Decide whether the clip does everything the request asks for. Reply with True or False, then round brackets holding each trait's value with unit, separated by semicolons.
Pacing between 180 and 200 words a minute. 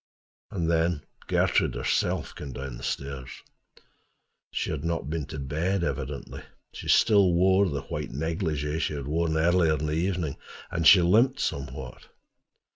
False (150 wpm)